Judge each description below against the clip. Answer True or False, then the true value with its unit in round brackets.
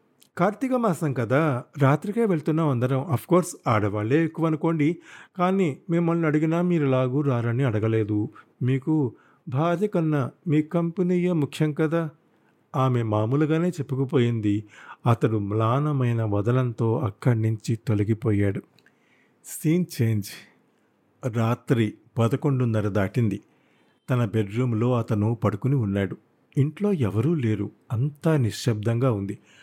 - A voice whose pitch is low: True (130 Hz)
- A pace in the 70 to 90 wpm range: False (100 wpm)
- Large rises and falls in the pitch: True (5.9 semitones)